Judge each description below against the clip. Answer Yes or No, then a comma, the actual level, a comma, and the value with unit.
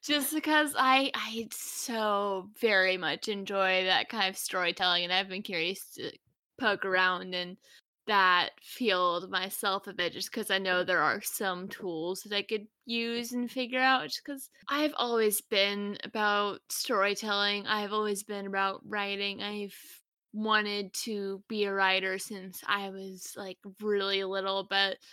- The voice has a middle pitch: No, high, 200 Hz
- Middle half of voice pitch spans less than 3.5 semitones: Yes, narrow, 2.6 semitones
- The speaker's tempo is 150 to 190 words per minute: Yes, average, 155 wpm